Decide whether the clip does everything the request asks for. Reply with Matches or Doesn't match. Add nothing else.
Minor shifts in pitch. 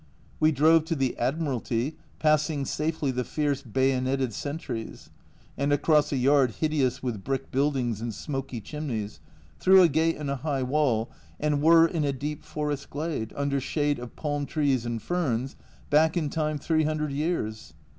Doesn't match